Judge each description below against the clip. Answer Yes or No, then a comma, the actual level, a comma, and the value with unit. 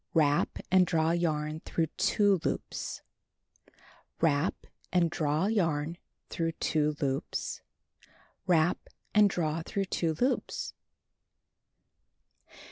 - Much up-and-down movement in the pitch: No, average, 3.0 semitones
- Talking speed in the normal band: No, slow, 110 wpm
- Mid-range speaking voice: Yes, medium, 165 Hz